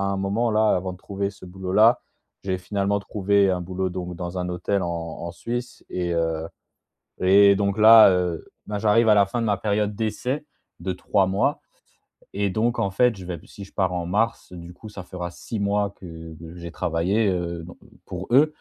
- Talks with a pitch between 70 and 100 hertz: Yes, very low, 95 Hz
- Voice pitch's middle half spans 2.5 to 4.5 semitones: Yes, average, 2.8 semitones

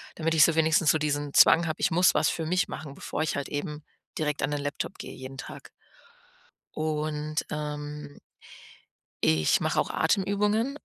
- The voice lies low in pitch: No, medium, 150 Hz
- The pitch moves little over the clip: Yes, narrow, 1.8 semitones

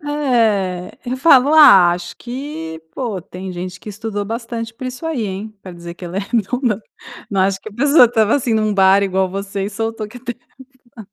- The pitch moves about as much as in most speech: Yes, average, 4.3 semitones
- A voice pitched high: Yes, high, 215 Hz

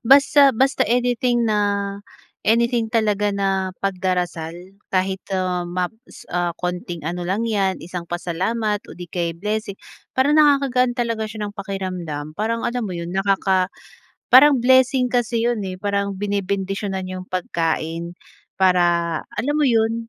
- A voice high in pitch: Yes, high, 200 Hz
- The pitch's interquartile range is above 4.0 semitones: Yes, average, 4.4 semitones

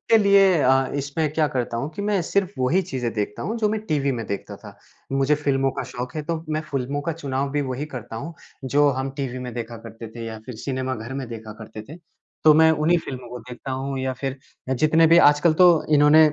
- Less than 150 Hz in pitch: Yes, low, 135 Hz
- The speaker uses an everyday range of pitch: Yes, average, 3.7 semitones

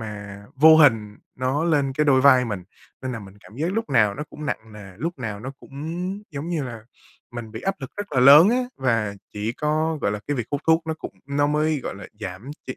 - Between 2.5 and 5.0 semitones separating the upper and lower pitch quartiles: No, wide, 5.6 semitones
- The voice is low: Yes, low, 130 Hz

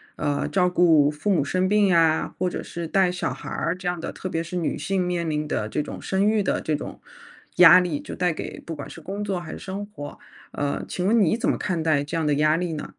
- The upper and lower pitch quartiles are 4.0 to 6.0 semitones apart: No, average, 3.3 semitones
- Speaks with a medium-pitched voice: Yes, medium, 175 Hz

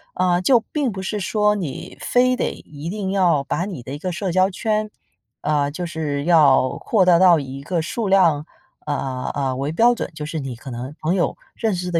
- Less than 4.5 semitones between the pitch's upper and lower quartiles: No, average, 5.2 semitones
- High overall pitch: No, medium, 170 Hz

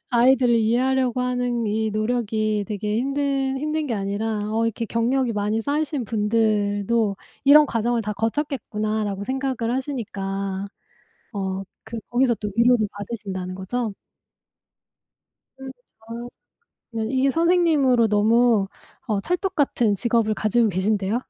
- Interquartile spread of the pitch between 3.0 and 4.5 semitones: Yes, average, 3.6 semitones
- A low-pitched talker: No, high, 230 Hz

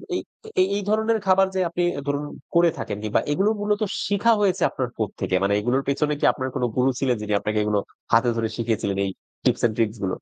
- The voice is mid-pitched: No, low, 130 Hz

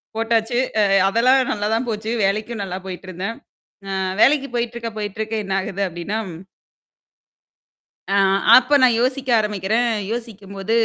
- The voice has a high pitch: Yes, high, 220 Hz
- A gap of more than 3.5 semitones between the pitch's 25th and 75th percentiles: No, average, 3.2 semitones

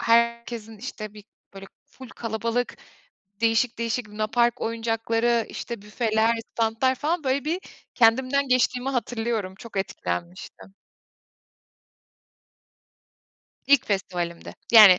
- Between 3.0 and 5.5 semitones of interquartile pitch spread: No, narrow, 2.4 semitones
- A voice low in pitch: No, high, 230 Hz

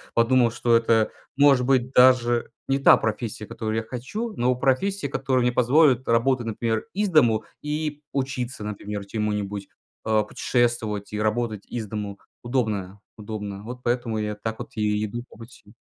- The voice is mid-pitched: No, low, 120 Hz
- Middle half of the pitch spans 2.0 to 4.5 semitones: Yes, average, 3.2 semitones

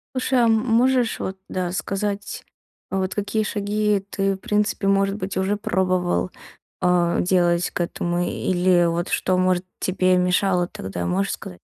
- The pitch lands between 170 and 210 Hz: Yes, medium, 185 Hz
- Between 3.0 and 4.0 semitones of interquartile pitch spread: No, narrow, 2.6 semitones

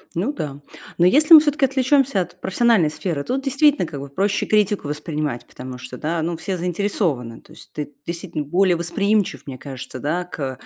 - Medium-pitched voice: Yes, medium, 175 Hz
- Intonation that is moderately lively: No, wide, 6.4 semitones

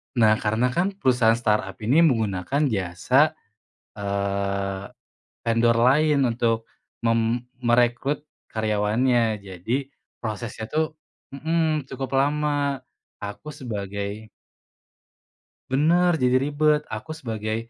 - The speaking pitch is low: Yes, low, 120 Hz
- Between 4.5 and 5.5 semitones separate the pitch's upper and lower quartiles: Yes, average, 4.9 semitones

